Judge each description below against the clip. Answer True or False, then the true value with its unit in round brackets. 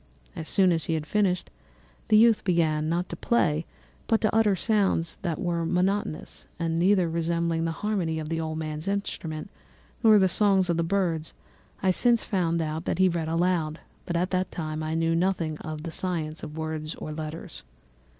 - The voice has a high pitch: False (170 Hz)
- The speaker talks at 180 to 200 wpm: True (185 wpm)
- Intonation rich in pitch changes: False (2.9 semitones)